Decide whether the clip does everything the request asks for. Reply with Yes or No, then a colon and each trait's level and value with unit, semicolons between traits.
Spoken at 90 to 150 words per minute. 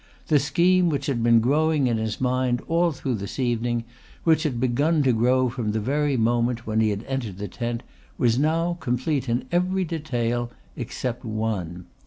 No: average, 180 wpm